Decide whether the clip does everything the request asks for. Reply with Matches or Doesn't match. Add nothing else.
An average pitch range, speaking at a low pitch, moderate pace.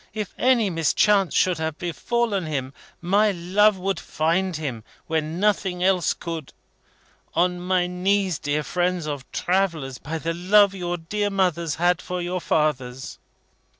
Doesn't match